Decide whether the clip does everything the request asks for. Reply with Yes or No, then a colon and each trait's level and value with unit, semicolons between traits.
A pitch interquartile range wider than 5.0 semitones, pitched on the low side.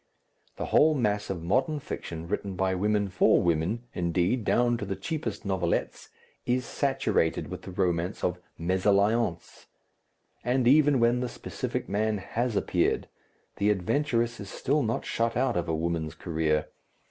Yes: wide, 5.4 semitones; low, 105 Hz